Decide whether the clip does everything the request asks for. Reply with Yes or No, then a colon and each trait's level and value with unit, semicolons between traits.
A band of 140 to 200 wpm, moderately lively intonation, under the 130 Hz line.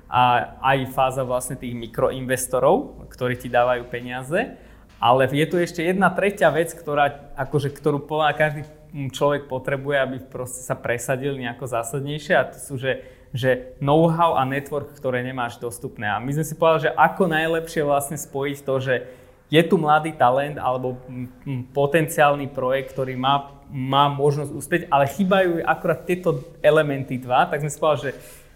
No: average, 160 wpm; average, 3.2 semitones; medium, 140 Hz